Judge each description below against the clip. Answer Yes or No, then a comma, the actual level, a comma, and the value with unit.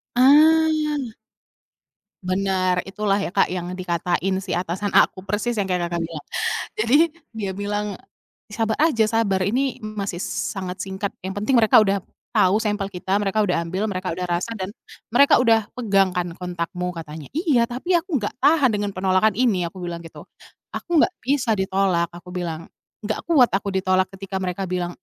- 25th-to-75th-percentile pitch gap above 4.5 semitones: No, average, 3.7 semitones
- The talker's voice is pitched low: No, high, 195 Hz